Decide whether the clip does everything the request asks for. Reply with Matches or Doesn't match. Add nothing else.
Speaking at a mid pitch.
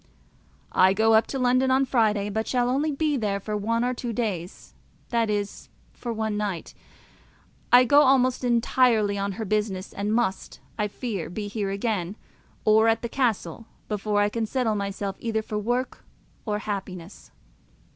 Doesn't match